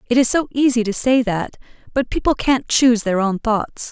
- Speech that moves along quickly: Yes, fast, 215 wpm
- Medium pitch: No, high, 235 Hz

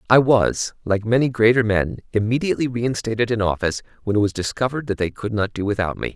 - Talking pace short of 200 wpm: No, fast, 205 wpm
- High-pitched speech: No, low, 110 Hz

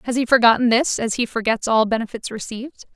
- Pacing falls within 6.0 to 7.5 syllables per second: Yes, 6.2 syllables/s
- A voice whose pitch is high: Yes, high, 235 Hz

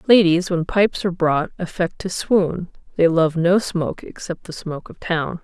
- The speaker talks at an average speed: Yes, average, 190 wpm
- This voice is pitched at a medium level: Yes, medium, 175 Hz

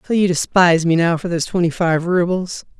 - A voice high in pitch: No, medium, 175 Hz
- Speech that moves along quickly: Yes, fast, 215 wpm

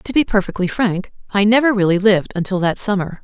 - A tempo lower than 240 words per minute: Yes, fast, 205 wpm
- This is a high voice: Yes, high, 200 Hz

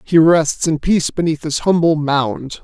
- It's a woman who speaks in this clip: No, male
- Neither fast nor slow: Yes, average, 180 wpm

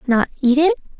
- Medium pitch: No, very high, 280 Hz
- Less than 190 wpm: Yes, average, 180 wpm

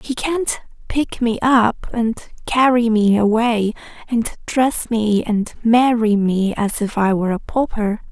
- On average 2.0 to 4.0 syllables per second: Yes, 3.8 syllables/s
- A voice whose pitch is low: No, high, 225 Hz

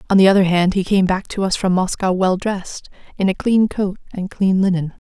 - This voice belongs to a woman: Yes, female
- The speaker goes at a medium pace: No, fast, 235 wpm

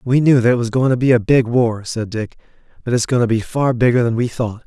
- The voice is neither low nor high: No, low, 120 Hz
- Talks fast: Yes, fast, 295 wpm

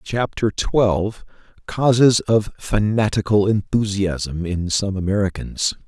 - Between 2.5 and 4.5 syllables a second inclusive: Yes, 3.8 syllables/s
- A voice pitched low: Yes, low, 105 Hz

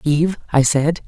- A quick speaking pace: No, average, 170 wpm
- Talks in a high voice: No, medium, 155 Hz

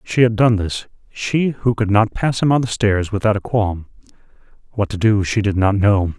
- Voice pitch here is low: Yes, low, 105 Hz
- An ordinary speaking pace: No, fast, 215 wpm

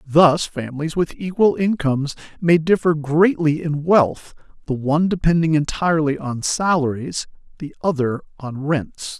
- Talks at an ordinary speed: No, slow, 130 wpm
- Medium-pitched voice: Yes, medium, 155 Hz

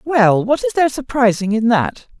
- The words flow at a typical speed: Yes, average, 190 wpm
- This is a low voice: No, high, 240 Hz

